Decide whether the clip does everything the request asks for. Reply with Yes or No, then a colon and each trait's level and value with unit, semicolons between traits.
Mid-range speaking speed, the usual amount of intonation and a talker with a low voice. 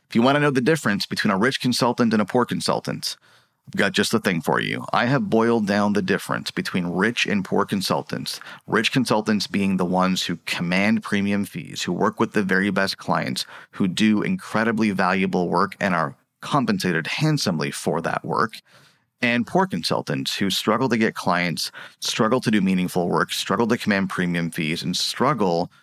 Yes: average, 190 wpm; average, 3.8 semitones; low, 105 Hz